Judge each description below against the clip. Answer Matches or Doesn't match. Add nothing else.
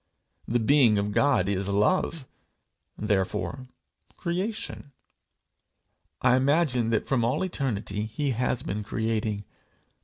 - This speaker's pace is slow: Matches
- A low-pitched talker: Matches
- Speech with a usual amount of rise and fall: Matches